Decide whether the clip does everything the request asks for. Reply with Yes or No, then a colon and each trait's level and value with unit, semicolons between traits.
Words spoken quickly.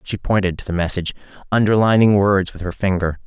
No: average, 185 wpm